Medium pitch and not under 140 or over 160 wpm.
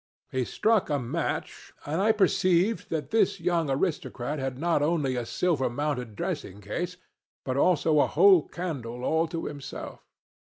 Yes: medium, 155 Hz; average, 155 wpm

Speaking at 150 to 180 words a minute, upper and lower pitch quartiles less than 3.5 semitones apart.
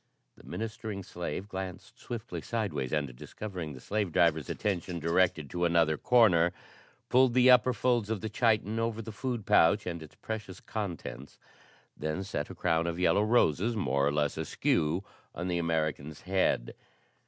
No: average, 160 wpm; average, 5.3 semitones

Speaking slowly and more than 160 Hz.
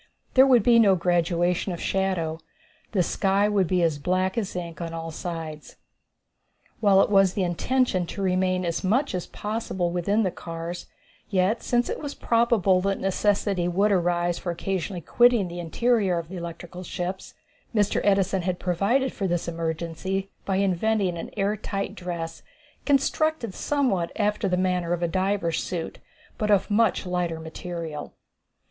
No: average, 160 wpm; medium, 185 Hz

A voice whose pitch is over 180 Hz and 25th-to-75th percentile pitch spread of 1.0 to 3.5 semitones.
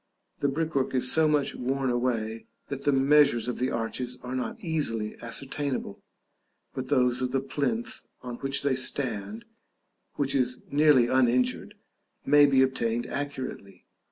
No: low, 130 Hz; narrow, 2.5 semitones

